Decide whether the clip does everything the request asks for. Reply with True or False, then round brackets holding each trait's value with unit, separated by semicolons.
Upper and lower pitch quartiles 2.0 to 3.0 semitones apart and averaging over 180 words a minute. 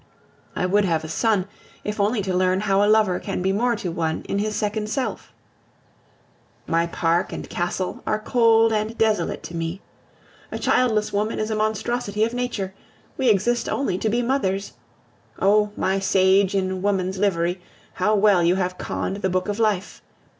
False (2.7 semitones; 175 wpm)